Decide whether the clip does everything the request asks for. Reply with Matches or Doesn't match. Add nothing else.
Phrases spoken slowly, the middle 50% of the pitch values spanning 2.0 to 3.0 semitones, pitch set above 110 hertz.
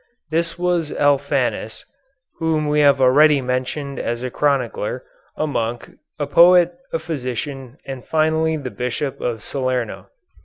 Doesn't match